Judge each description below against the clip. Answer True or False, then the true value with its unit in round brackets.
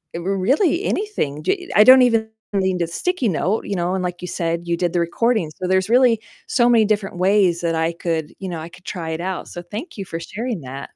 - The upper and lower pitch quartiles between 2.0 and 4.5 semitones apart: False (5.1 semitones)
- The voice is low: False (190 Hz)